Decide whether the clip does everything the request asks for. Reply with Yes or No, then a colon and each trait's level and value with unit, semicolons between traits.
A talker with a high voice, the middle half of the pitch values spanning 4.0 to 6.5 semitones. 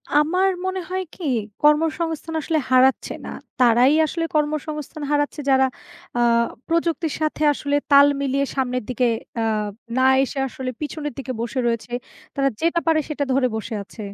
No: very high, 290 Hz; average, 3.4 semitones